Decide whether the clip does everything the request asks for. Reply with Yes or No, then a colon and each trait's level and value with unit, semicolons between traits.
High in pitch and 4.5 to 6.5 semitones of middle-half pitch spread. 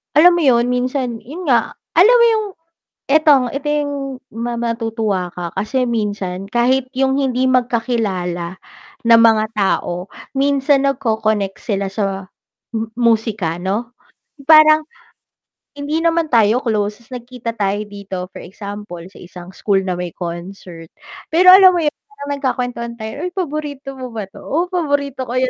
Yes: high, 235 Hz; wide, 5.6 semitones